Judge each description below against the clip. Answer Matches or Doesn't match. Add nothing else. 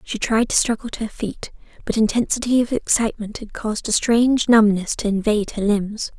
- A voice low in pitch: Doesn't match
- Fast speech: Doesn't match